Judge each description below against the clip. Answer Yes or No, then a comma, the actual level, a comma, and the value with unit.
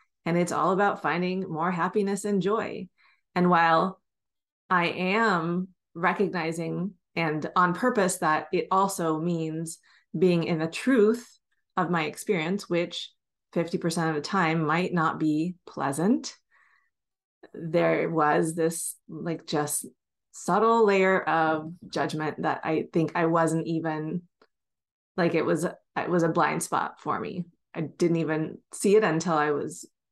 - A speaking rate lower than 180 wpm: Yes, average, 140 wpm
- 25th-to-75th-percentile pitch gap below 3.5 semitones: Yes, average, 2.8 semitones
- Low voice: No, medium, 170 Hz